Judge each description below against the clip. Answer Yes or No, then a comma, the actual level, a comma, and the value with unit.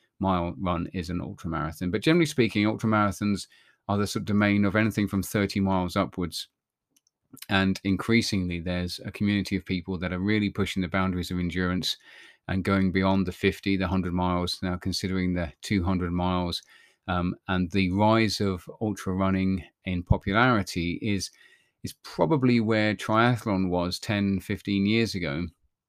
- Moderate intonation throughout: No, narrow, 2.3 semitones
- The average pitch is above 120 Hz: No, very low, 95 Hz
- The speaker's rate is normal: Yes, average, 160 wpm